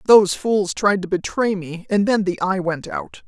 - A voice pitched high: Yes, high, 195 Hz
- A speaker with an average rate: No, fast, 220 wpm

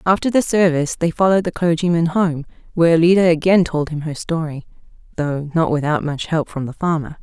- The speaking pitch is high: No, medium, 165 Hz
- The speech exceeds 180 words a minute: Yes, average, 190 wpm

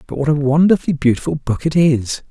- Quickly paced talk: Yes, fast, 210 wpm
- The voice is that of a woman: No, male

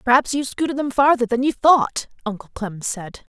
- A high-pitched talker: Yes, very high, 250 Hz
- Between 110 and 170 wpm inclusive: No, average, 195 wpm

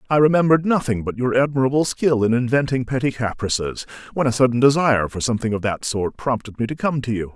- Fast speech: Yes, fast, 210 wpm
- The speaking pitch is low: Yes, low, 125 Hz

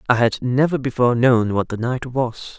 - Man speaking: Yes, male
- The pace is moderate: No, fast, 210 wpm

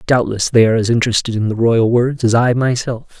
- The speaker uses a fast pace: Yes, fast, 225 wpm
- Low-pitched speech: Yes, low, 115 Hz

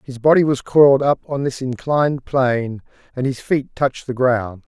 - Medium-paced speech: Yes, average, 190 wpm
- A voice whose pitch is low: Yes, low, 130 Hz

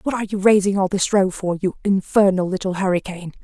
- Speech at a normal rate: No, fast, 210 wpm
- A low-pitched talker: No, high, 190 Hz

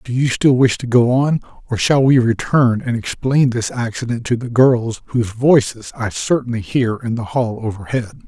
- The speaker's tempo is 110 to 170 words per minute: No, average, 195 wpm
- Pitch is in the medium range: No, low, 120 Hz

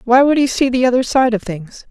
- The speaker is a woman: Yes, female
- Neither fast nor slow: No, fast, 285 wpm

